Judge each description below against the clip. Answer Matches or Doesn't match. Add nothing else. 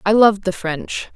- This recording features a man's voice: Doesn't match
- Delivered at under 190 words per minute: Doesn't match